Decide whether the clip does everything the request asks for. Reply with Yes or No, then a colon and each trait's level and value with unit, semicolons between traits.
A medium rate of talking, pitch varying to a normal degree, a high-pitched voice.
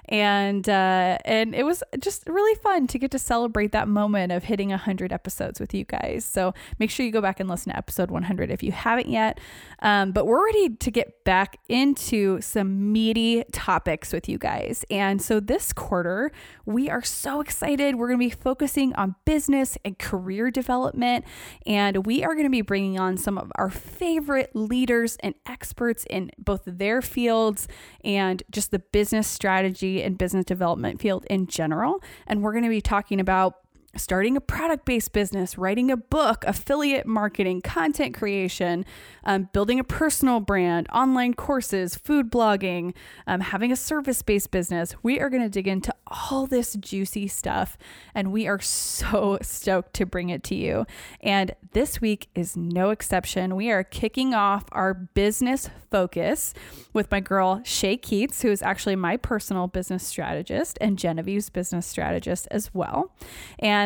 Yes: average, 170 wpm; average, 4.5 semitones; high, 210 Hz